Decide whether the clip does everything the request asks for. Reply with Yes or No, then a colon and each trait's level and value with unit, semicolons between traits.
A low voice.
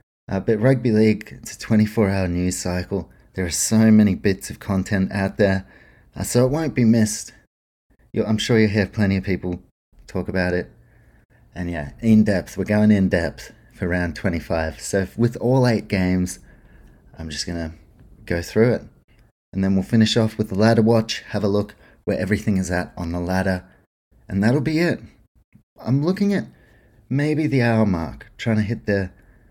Yes: low, 100 Hz